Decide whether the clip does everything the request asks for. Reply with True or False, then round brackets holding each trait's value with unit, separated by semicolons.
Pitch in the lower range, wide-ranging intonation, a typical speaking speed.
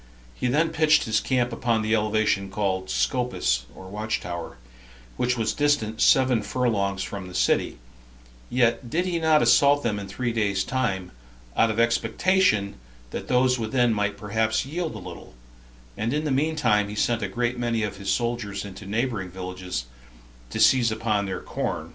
False (110 Hz; 3.8 semitones; 175 wpm)